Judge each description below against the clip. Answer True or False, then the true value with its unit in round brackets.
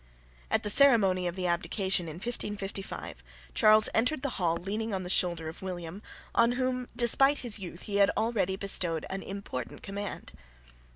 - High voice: True (195 Hz)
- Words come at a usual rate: True (165 wpm)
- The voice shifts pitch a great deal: False (3.9 semitones)